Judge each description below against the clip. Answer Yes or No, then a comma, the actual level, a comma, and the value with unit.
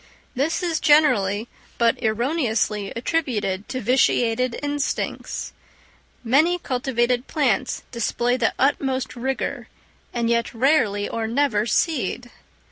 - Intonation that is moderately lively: Yes, average, 3.6 semitones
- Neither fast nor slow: No, slow, 105 wpm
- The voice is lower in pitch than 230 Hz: No, high, 245 Hz